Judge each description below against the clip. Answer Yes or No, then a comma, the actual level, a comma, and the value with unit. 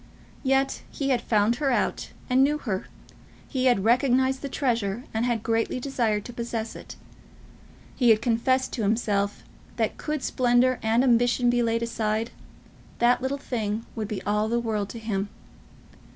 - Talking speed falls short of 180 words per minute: Yes, average, 165 wpm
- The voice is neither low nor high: No, high, 235 Hz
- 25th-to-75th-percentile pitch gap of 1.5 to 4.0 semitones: Yes, average, 2.7 semitones